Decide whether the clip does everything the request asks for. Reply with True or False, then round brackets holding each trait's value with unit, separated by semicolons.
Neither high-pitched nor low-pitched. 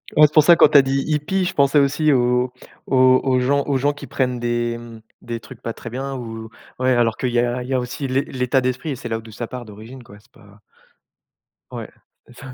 False (125 Hz)